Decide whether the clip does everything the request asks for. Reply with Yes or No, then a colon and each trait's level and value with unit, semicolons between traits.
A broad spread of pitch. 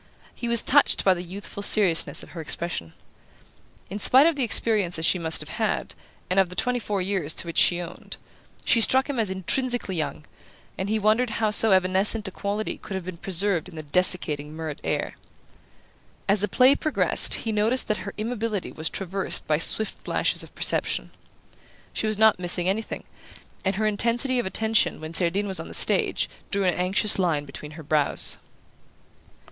No: average, 4.0 semitones